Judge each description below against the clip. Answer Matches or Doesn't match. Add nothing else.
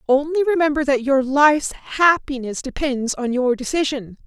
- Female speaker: Matches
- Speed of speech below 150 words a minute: Matches